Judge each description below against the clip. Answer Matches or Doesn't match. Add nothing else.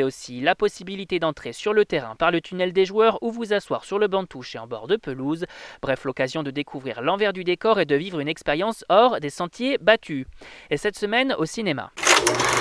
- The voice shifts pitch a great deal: Matches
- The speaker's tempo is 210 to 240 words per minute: Matches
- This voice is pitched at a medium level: Matches